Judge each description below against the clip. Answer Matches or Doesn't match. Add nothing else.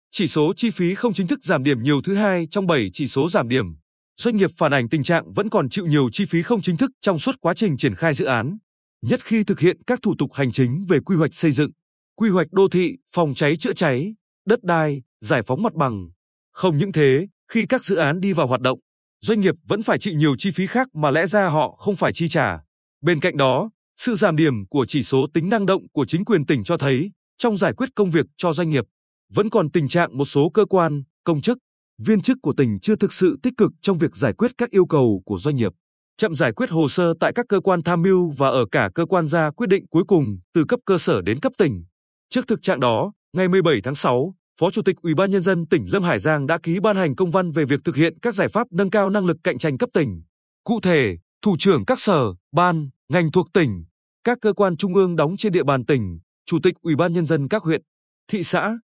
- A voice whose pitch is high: Doesn't match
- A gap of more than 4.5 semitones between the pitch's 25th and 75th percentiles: Matches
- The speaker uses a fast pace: Matches